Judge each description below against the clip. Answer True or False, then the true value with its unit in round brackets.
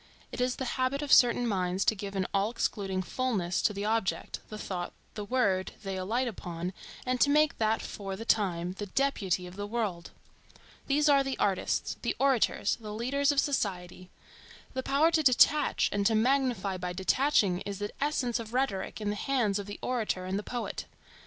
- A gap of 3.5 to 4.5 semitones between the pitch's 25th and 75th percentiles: False (5.1 semitones)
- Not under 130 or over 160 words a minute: False (190 wpm)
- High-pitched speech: True (215 Hz)